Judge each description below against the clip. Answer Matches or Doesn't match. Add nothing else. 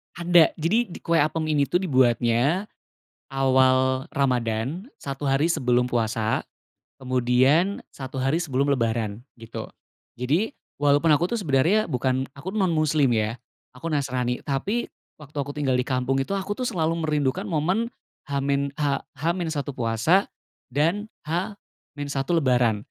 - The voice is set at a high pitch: Doesn't match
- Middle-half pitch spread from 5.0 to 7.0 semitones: Doesn't match